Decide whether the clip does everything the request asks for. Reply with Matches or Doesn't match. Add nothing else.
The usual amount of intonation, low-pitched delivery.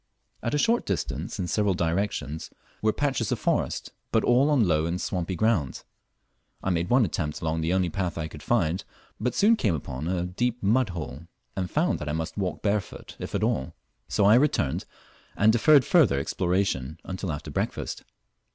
Doesn't match